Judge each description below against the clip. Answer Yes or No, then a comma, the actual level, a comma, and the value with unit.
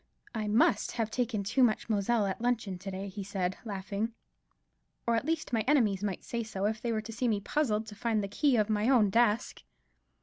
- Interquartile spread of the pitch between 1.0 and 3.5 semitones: Yes, average, 2.8 semitones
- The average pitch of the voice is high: Yes, high, 215 Hz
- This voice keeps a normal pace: No, fast, 215 wpm